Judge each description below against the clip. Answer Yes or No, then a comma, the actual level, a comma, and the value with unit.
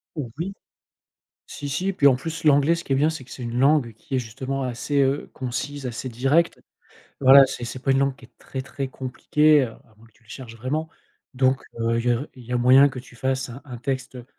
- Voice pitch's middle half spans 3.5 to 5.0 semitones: No, narrow, 2.6 semitones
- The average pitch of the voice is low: Yes, low, 130 Hz